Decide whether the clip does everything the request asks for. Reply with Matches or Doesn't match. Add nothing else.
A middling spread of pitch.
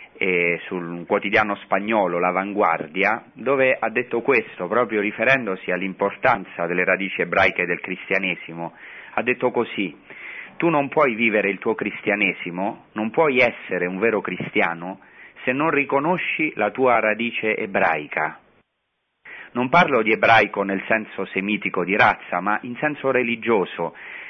Matches